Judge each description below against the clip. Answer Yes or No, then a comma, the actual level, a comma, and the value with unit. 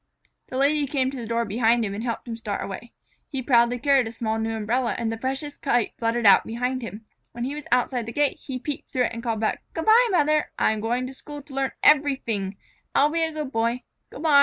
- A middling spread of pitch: Yes, average, 3.6 semitones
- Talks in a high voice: Yes, high, 245 Hz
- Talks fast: Yes, fast, 240 wpm